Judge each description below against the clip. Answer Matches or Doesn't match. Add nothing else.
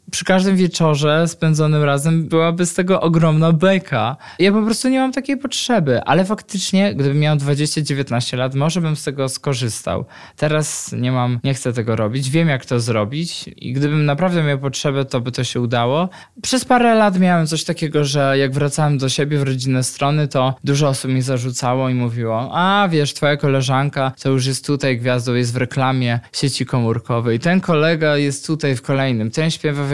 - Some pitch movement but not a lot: Matches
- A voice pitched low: Doesn't match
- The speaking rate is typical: Doesn't match